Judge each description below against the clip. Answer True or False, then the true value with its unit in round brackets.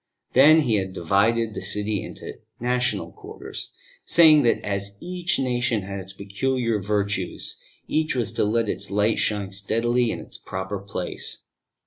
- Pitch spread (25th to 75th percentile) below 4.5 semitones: True (3.8 semitones)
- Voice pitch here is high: False (105 Hz)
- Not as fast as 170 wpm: True (150 wpm)